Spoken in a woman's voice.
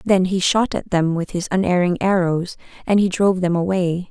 Yes: female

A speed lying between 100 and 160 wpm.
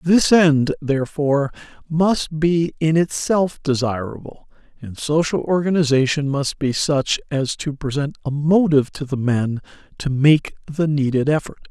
Yes: average, 140 wpm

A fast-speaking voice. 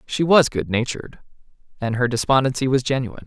No: average, 145 wpm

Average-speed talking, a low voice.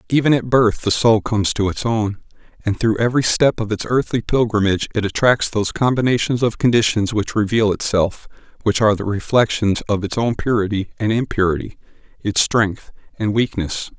Yes: average, 170 wpm; low, 110 Hz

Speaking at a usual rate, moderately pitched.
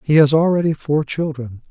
Yes: average, 175 wpm; medium, 150 Hz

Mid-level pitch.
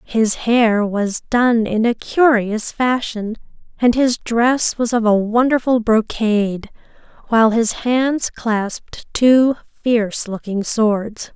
No: high, 230 Hz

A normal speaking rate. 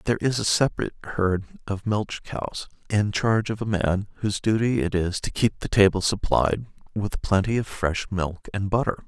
Yes: average, 190 wpm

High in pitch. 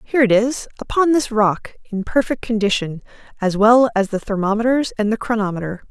Yes: high, 220 Hz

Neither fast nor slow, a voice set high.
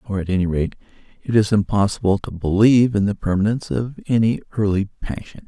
No: average, 175 wpm; low, 105 Hz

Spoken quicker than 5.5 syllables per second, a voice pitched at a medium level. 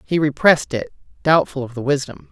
Yes: 5.9 syllables/s; medium, 145 Hz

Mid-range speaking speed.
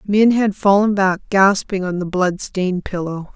Yes: average, 180 wpm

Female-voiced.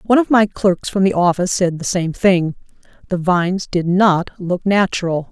Yes: female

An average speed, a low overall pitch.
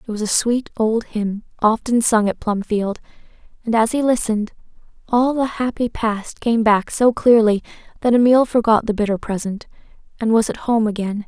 No: average, 175 wpm; high, 225 Hz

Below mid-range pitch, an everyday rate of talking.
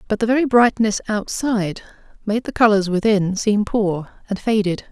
No: high, 210 Hz; average, 160 wpm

